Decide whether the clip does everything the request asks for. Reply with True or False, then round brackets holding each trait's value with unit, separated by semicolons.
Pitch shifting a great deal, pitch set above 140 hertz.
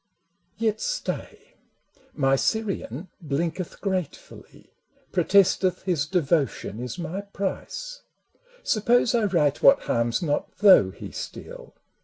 True (6.1 semitones; 185 Hz)